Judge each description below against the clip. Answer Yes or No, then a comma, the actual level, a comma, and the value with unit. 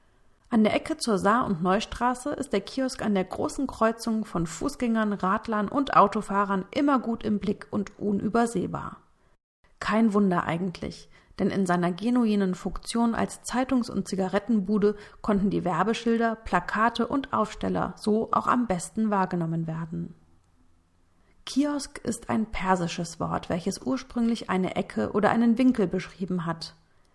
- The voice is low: No, high, 205 Hz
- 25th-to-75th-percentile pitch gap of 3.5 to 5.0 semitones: Yes, average, 4.0 semitones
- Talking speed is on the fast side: No, average, 140 wpm